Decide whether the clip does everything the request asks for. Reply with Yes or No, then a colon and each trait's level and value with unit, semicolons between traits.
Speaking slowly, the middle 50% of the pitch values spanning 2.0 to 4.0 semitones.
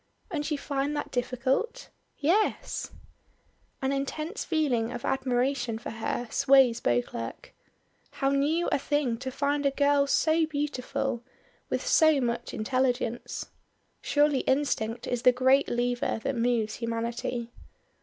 Yes: slow, 125 wpm; average, 3.3 semitones